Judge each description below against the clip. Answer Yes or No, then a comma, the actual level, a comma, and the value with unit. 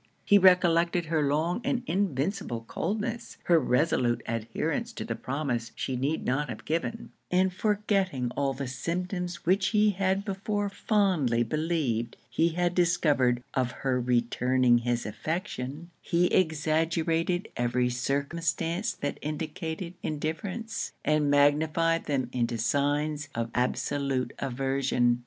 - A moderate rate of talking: No, slow, 125 wpm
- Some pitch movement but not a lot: No, wide, 5.7 semitones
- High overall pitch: No, medium, 155 Hz